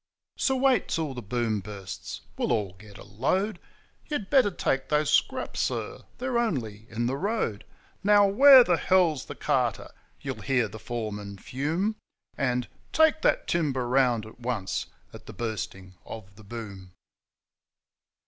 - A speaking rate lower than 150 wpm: No, average, 155 wpm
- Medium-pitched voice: No, low, 125 Hz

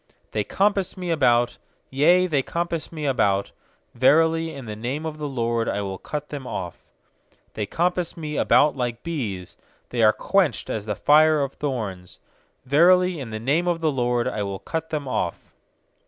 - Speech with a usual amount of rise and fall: No, wide, 5.8 semitones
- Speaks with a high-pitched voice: No, medium, 140 Hz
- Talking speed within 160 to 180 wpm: Yes, average, 175 wpm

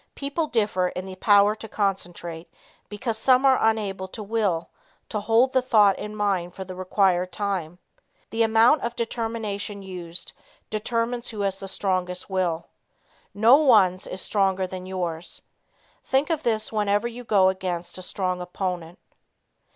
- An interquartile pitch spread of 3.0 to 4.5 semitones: Yes, average, 3.4 semitones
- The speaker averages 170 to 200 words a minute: No, average, 150 wpm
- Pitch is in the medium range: No, high, 200 Hz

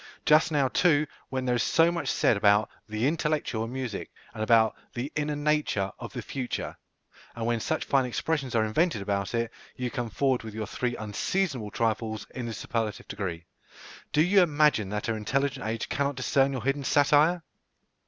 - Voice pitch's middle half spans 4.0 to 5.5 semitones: Yes, average, 4.9 semitones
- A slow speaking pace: No, average, 185 wpm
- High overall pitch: No, low, 125 Hz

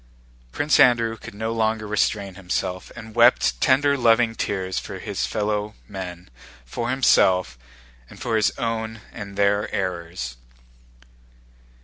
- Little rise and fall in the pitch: No, average, 3.5 semitones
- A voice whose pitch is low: Yes, low, 105 Hz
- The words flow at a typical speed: No, slow, 125 wpm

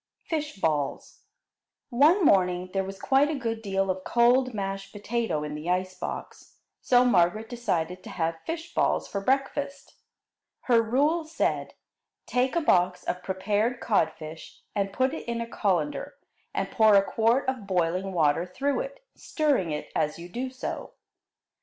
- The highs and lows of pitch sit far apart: Yes, wide, 6.2 semitones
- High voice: Yes, high, 210 Hz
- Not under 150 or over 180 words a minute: Yes, average, 160 wpm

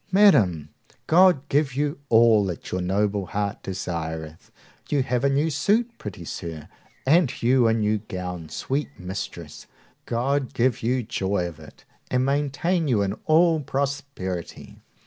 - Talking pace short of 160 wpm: Yes, average, 145 wpm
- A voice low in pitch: Yes, low, 120 Hz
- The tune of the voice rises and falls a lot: Yes, wide, 7.4 semitones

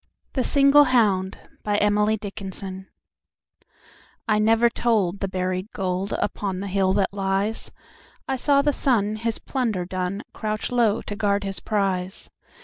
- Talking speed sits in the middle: No, slow, 120 wpm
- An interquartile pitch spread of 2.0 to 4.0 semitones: Yes, average, 2.8 semitones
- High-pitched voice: Yes, high, 205 Hz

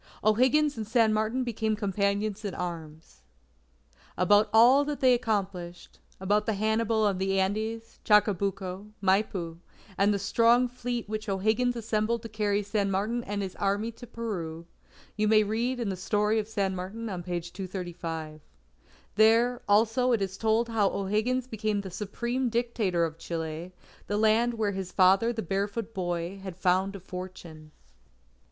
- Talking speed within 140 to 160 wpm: Yes, average, 155 wpm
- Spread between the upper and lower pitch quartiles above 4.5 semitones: No, average, 3.2 semitones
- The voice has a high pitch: Yes, high, 210 Hz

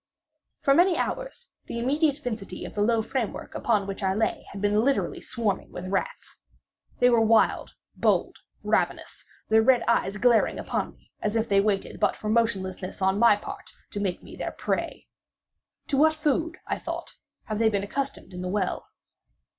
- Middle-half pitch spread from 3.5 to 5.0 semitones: Yes, average, 4.5 semitones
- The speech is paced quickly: No, average, 175 wpm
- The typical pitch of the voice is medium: No, high, 220 Hz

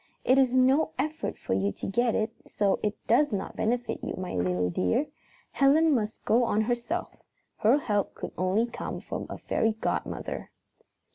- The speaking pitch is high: Yes, high, 225 Hz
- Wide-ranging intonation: No, average, 4.3 semitones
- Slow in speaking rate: No, average, 170 wpm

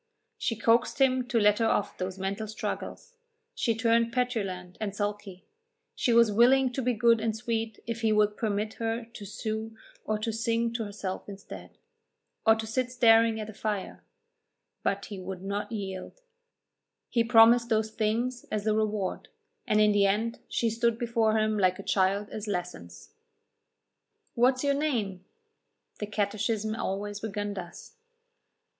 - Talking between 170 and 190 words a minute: No, average, 160 wpm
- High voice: Yes, high, 220 Hz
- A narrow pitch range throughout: Yes, narrow, 2.2 semitones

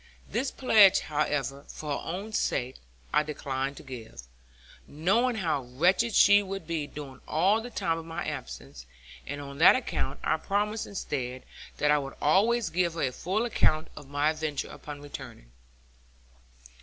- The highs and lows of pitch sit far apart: Yes, wide, 5.8 semitones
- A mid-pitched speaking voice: Yes, medium, 155 Hz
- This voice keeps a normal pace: Yes, average, 160 wpm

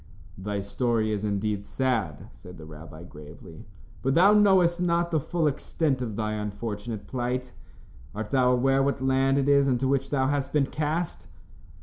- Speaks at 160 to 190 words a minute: Yes, average, 165 wpm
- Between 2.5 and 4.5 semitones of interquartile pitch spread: No, average, 5.1 semitones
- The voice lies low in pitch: Yes, low, 130 Hz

